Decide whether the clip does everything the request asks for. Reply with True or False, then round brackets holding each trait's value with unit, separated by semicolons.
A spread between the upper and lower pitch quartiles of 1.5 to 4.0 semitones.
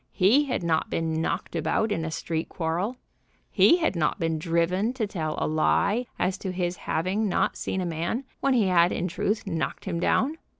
False (4.5 semitones)